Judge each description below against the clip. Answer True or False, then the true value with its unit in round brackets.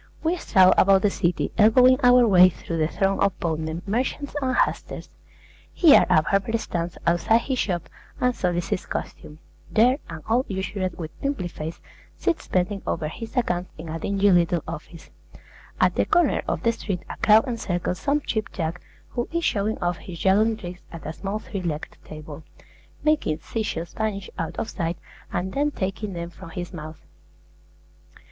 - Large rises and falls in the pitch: False (4.9 semitones)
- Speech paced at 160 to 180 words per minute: True (175 wpm)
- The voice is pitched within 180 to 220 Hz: True (190 Hz)